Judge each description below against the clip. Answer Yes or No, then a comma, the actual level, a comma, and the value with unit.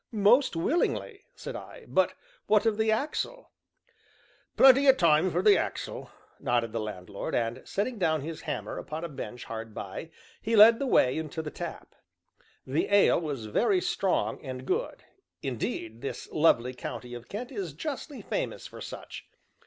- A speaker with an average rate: Yes, average, 160 wpm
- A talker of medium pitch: Yes, medium, 170 Hz